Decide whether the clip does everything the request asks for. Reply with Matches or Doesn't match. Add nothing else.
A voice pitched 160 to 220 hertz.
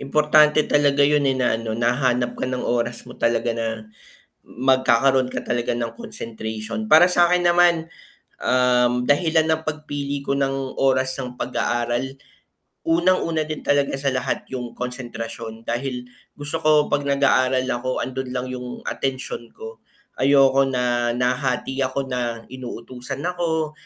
Doesn't match